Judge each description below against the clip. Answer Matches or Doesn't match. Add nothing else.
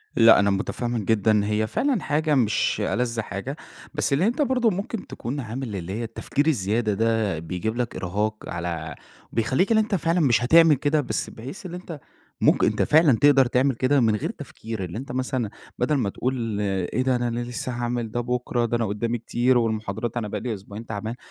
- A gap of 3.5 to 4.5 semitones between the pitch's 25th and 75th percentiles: Matches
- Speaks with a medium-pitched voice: Doesn't match